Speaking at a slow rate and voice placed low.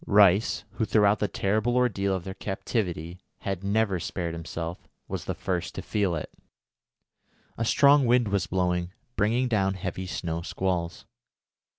No: average, 150 wpm; very low, 95 Hz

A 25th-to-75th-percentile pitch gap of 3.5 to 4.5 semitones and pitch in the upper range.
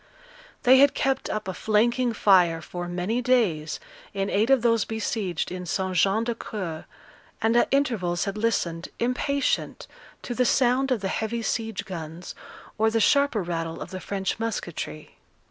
No: average, 4.9 semitones; high, 215 Hz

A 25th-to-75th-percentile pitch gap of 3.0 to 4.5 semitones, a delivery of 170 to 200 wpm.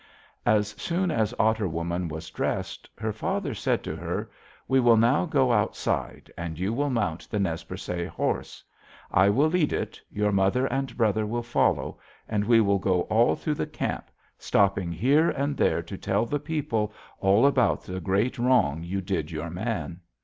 No: wide, 5.4 semitones; average, 180 wpm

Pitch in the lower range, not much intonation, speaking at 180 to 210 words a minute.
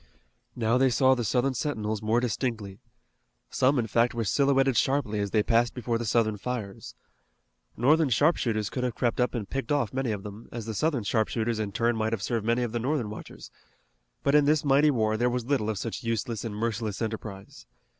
No: low, 115 Hz; average, 3.0 semitones; fast, 205 wpm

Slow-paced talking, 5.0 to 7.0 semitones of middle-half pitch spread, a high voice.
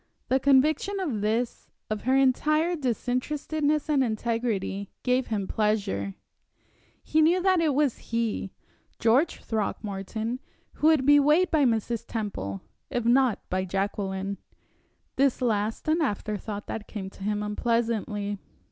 Yes: slow, 130 wpm; wide, 5.5 semitones; high, 235 Hz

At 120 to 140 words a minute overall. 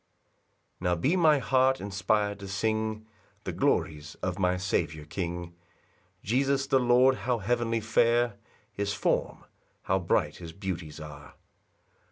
Yes: slow, 135 wpm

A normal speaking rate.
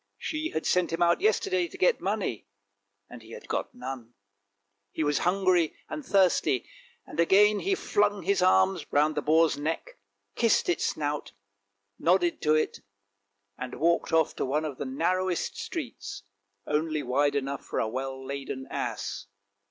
Yes: average, 160 wpm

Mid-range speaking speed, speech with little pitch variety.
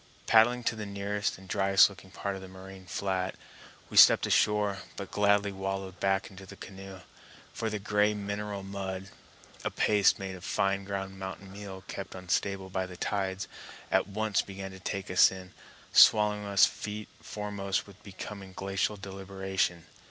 Yes: average, 165 wpm; narrow, 1.2 semitones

